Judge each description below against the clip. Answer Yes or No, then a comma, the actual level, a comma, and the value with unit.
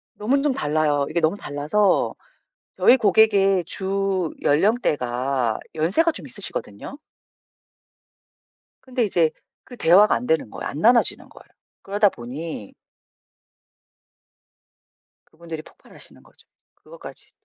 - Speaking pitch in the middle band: Yes, medium, 180 Hz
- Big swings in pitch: Yes, wide, 5.7 semitones